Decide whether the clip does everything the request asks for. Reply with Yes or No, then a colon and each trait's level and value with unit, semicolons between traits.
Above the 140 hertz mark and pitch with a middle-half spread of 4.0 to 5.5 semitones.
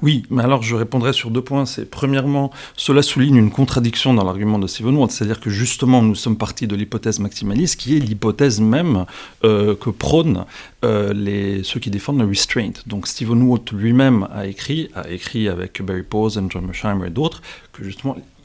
No: low, 115 Hz; average, 4.6 semitones